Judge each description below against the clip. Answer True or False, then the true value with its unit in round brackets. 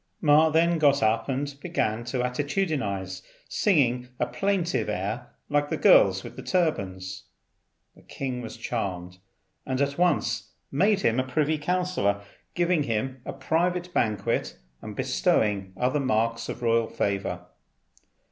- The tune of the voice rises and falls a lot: True (6.5 semitones)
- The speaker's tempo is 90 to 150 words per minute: True (140 wpm)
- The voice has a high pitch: False (130 Hz)